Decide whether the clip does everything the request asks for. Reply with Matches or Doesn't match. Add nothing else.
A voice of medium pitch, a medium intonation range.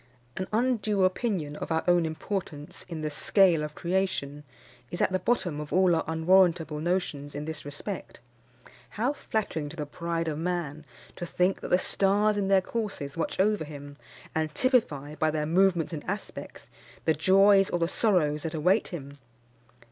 Matches